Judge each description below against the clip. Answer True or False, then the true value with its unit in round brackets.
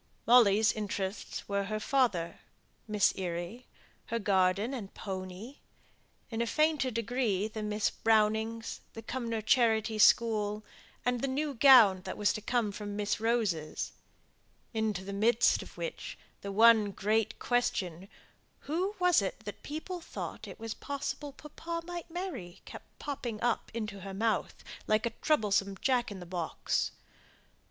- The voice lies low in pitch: False (220 Hz)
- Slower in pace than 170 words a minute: True (145 wpm)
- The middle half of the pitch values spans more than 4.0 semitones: False (3.6 semitones)